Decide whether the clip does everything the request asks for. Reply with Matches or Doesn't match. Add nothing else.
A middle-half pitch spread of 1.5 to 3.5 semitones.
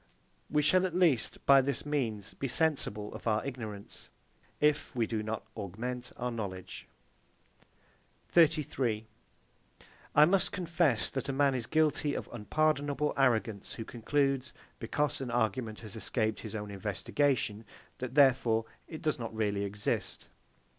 Doesn't match